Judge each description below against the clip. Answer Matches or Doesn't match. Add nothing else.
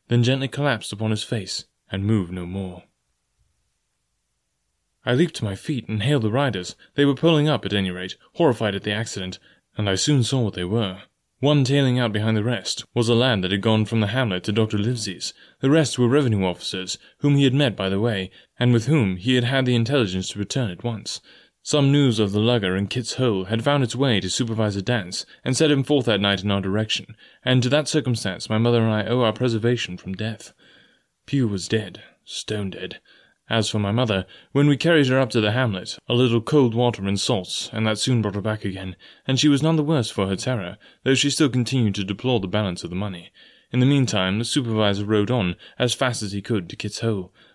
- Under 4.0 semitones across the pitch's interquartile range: Doesn't match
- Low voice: Matches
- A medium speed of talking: Doesn't match